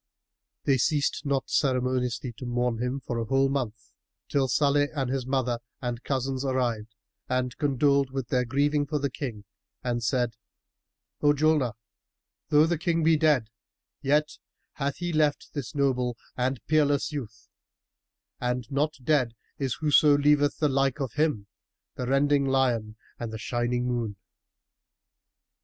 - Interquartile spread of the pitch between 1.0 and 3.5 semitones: Yes, average, 2.8 semitones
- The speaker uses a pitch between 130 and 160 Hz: Yes, low, 135 Hz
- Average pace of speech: Yes, average, 145 wpm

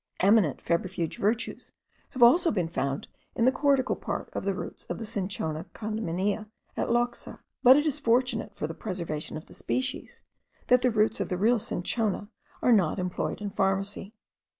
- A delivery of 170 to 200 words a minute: Yes, average, 175 wpm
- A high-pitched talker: Yes, high, 210 Hz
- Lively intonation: No, average, 4.7 semitones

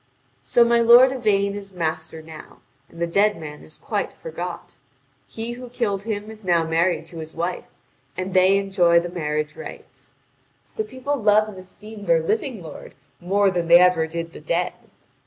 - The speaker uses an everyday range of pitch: Yes, average, 4.7 semitones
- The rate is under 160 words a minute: No, average, 175 wpm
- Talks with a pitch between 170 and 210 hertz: Yes, high, 190 Hz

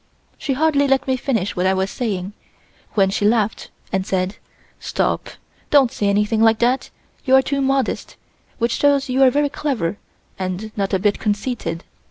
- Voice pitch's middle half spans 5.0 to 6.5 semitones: Yes, wide, 5.4 semitones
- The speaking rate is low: No, average, 175 wpm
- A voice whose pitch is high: Yes, high, 225 Hz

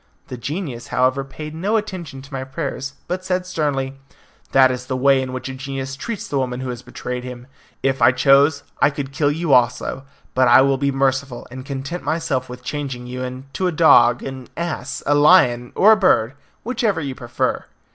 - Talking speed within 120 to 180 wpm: No, average, 195 wpm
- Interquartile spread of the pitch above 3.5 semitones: No, average, 2.9 semitones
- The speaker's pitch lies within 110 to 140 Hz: Yes, low, 135 Hz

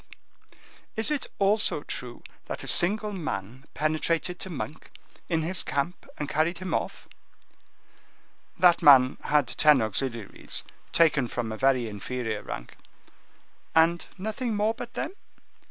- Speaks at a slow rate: Yes, slow, 130 wpm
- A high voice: No, medium, 155 Hz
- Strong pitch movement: Yes, wide, 6.5 semitones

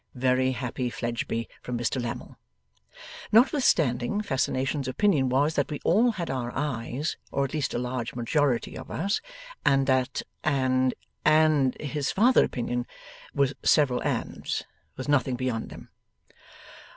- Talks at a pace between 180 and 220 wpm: No, slow, 135 wpm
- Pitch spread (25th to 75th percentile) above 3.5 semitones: No, average, 3.2 semitones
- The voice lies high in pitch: No, low, 130 Hz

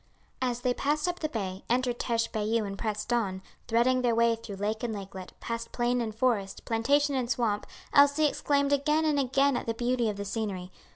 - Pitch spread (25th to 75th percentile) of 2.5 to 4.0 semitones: Yes, average, 3.5 semitones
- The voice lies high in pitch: Yes, high, 235 Hz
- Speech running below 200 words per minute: No, fast, 205 wpm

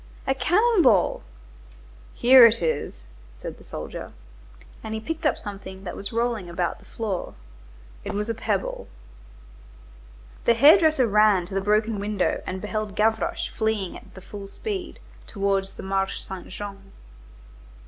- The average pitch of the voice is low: No, high, 210 Hz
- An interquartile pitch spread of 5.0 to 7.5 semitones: No, average, 3.1 semitones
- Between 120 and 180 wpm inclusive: Yes, average, 150 wpm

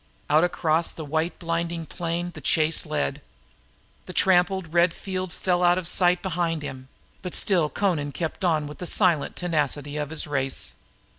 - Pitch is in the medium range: Yes, medium, 165 Hz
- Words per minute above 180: No, average, 165 wpm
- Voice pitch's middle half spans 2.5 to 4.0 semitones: Yes, average, 2.8 semitones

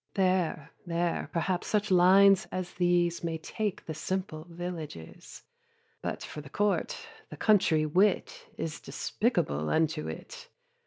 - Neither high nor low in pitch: Yes, medium, 175 Hz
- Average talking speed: No, slow, 125 wpm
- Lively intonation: No, average, 3.1 semitones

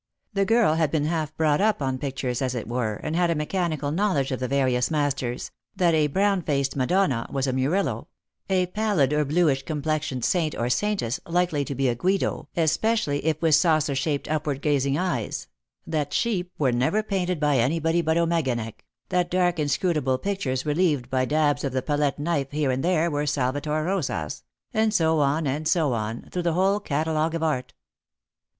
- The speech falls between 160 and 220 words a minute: Yes, average, 185 wpm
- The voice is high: No, medium, 150 Hz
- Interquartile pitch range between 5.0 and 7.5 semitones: No, average, 4.3 semitones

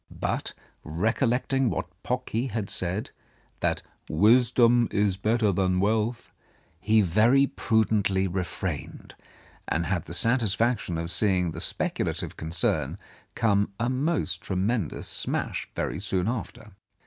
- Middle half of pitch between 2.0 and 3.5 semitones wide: No, average, 4.3 semitones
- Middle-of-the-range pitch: No, low, 105 Hz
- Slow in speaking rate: Yes, slow, 115 wpm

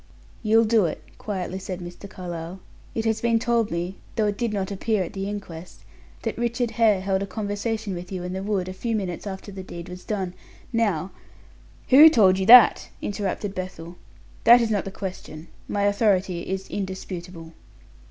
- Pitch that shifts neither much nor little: Yes, average, 3.0 semitones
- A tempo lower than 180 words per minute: No, average, 185 wpm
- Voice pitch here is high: Yes, high, 195 Hz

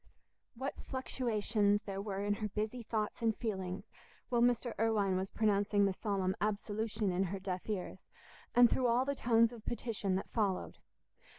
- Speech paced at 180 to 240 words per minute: No, average, 165 wpm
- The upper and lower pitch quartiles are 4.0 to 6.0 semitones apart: No, average, 2.7 semitones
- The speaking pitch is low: No, high, 210 Hz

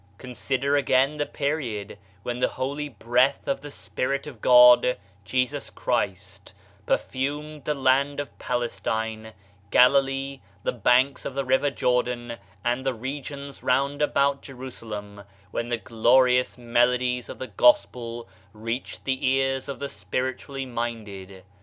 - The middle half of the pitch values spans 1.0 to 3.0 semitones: Yes, narrow, 2.5 semitones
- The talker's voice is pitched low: Yes, low, 130 Hz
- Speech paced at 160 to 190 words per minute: No, average, 140 wpm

